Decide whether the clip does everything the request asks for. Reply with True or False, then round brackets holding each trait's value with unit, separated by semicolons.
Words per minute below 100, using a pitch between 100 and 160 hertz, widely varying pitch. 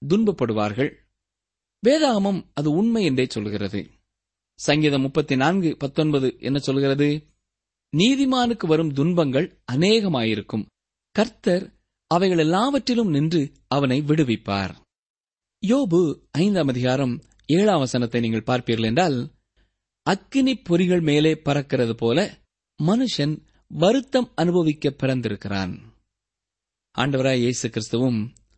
True (90 wpm; 140 Hz; 7.8 semitones)